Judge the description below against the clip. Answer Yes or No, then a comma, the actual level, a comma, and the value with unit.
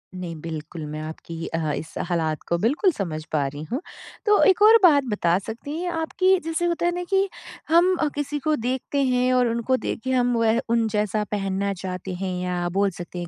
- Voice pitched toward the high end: Yes, high, 225 Hz